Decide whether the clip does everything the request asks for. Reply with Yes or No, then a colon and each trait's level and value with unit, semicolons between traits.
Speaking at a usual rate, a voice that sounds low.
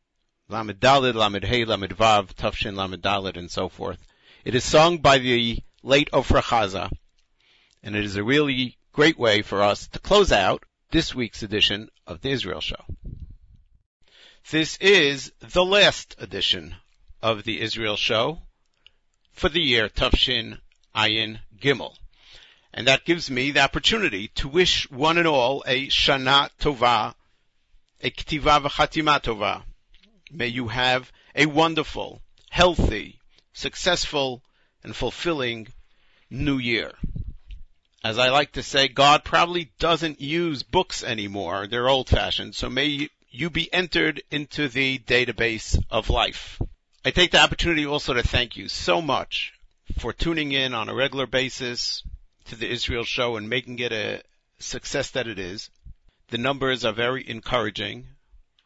Yes: average, 145 wpm; low, 125 Hz